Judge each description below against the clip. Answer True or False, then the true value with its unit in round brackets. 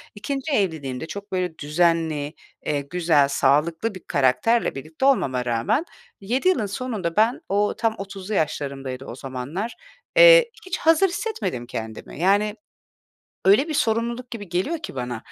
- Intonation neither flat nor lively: False (8.4 semitones)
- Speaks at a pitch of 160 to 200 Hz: True (185 Hz)